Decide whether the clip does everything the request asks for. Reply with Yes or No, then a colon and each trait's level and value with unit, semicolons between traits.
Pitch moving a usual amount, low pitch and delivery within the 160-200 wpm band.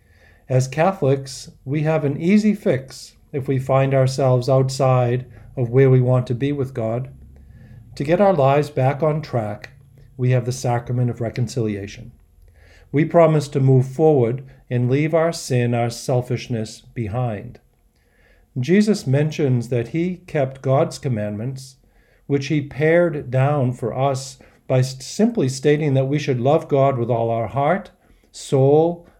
No: average, 3.3 semitones; low, 130 Hz; average, 145 wpm